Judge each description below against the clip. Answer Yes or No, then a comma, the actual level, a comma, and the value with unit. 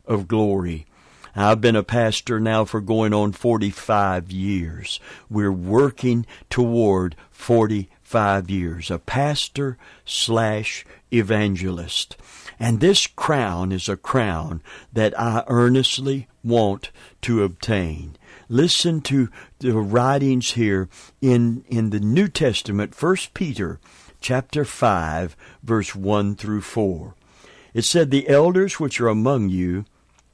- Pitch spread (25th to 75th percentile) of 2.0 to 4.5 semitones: Yes, average, 4.1 semitones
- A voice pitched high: No, low, 110 Hz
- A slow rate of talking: Yes, slow, 115 wpm